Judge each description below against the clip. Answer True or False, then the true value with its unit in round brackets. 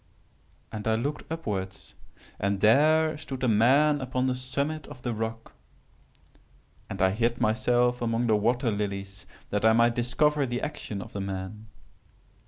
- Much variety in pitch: False (3.7 semitones)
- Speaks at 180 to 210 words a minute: False (155 wpm)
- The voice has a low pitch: True (120 Hz)